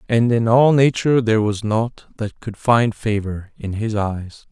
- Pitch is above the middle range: No, low, 110 Hz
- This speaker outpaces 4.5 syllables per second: No, 4.4 syllables/s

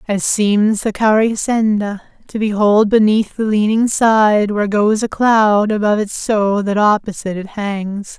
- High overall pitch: Yes, high, 210 Hz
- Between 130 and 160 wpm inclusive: Yes, average, 155 wpm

